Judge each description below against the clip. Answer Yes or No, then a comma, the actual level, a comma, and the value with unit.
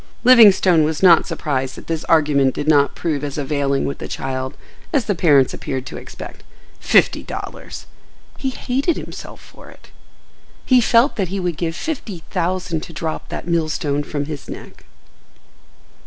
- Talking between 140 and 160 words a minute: Yes, average, 155 wpm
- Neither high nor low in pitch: Yes, medium, 160 Hz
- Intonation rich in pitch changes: No, average, 4.7 semitones